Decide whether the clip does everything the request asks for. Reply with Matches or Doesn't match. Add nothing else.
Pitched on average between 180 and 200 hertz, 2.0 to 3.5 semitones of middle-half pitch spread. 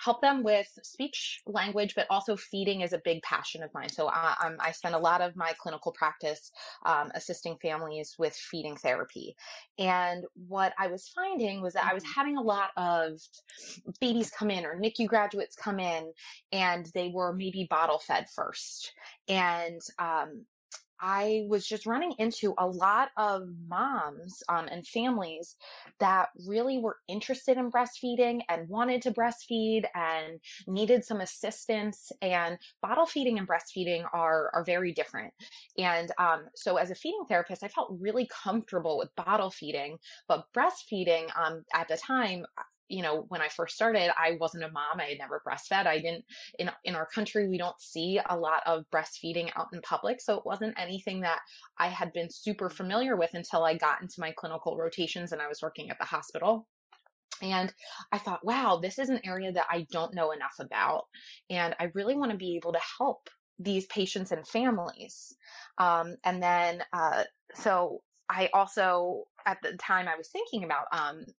Doesn't match